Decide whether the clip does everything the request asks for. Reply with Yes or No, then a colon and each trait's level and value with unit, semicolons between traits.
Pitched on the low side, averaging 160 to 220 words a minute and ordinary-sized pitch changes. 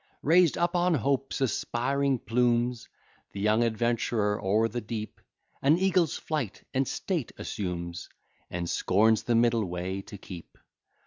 No: low, 115 Hz; slow, 135 wpm; average, 4.9 semitones